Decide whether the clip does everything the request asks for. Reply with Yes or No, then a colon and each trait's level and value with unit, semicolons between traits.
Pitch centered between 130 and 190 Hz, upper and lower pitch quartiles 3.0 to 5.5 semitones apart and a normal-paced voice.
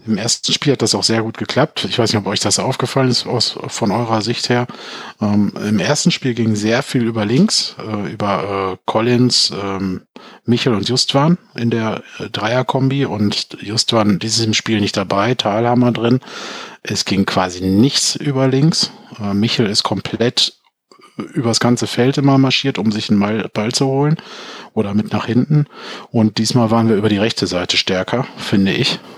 No: low, 115 Hz; average, 3.7 semitones; average, 170 wpm